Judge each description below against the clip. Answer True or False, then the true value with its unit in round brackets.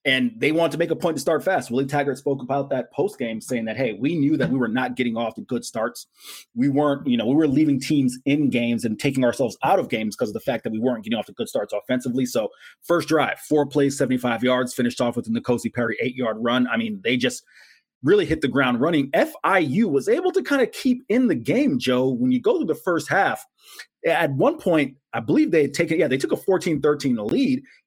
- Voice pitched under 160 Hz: True (140 Hz)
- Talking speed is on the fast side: True (255 wpm)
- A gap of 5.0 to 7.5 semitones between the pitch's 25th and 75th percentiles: True (5.5 semitones)